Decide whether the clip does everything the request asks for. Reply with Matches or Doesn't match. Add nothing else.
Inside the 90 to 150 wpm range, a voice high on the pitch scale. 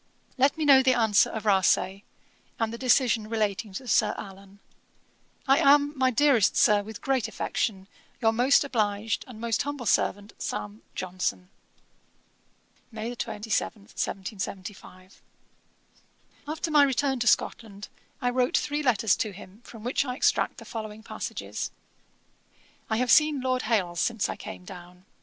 Matches